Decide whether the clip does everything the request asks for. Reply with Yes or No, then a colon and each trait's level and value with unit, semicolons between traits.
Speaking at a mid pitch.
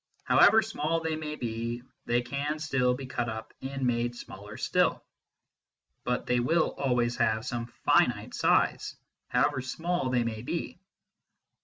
No: low, 125 Hz